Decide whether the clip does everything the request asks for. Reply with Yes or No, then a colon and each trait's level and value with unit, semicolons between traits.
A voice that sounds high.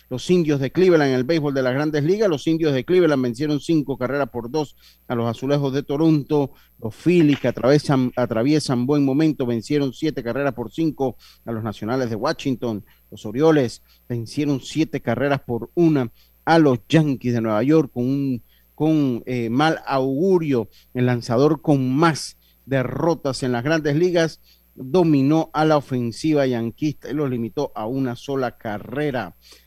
No: low, 135 Hz